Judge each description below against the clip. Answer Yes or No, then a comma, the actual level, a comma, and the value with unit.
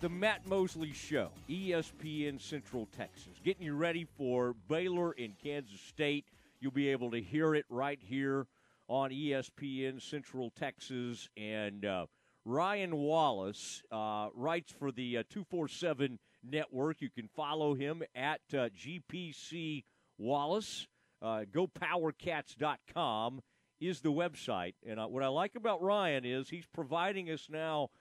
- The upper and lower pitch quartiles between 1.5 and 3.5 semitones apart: No, average, 4.7 semitones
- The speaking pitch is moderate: Yes, medium, 145 Hz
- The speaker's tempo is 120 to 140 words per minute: Yes, slow, 135 wpm